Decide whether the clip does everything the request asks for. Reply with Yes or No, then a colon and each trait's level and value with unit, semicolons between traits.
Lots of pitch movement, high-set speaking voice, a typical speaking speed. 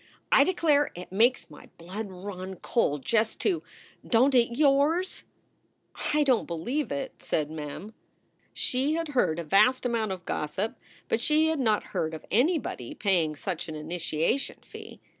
Yes: wide, 8.3 semitones; high, 220 Hz; average, 160 wpm